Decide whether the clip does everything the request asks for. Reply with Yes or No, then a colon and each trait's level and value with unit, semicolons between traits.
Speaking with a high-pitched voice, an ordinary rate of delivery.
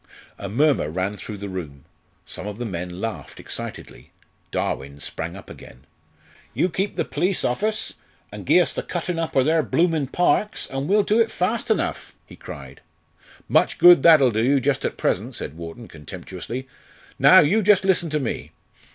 No: low, 135 Hz; average, 180 wpm